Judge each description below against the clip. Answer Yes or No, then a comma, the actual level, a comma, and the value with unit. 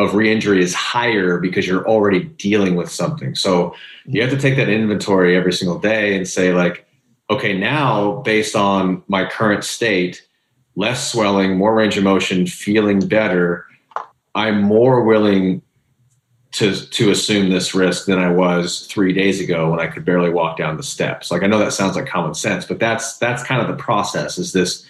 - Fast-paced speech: No, average, 185 wpm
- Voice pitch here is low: Yes, low, 100 Hz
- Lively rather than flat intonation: No, average, 3.1 semitones